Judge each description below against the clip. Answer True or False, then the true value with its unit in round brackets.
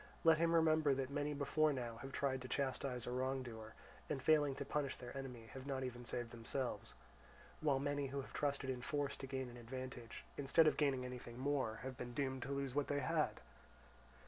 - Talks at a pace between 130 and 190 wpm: False (200 wpm)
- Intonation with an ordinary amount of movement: False (2.3 semitones)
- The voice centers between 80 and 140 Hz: True (135 Hz)